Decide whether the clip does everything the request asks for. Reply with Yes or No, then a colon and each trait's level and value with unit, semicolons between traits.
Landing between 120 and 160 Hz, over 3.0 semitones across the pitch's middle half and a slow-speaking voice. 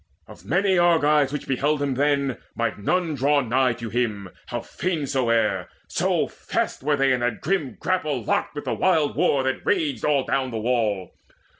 No: low, 135 Hz; average, 3.9 semitones; average, 180 wpm